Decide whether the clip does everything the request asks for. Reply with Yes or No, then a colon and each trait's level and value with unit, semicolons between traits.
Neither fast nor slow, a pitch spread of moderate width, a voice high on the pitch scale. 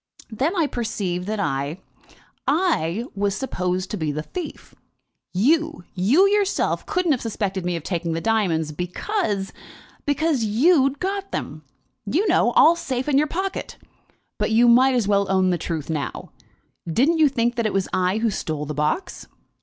No: average, 170 wpm; wide, 9.0 semitones; high, 220 Hz